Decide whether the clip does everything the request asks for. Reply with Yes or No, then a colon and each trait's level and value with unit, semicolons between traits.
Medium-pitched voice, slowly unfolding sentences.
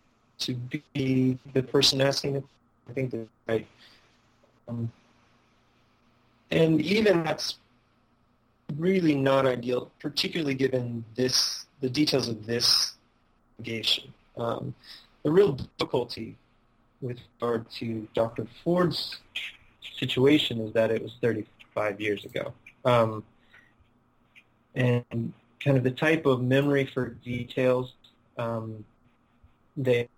No: low, 120 Hz; slow, 105 wpm